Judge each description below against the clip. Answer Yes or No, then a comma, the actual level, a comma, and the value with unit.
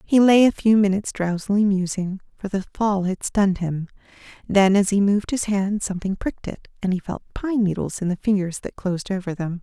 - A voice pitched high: Yes, high, 195 Hz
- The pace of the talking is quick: Yes, fast, 210 wpm